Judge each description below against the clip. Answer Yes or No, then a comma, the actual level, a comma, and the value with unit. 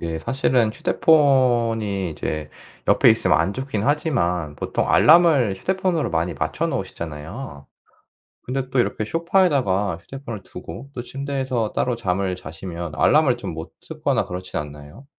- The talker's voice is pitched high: No, low, 115 Hz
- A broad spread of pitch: Yes, wide, 7.8 semitones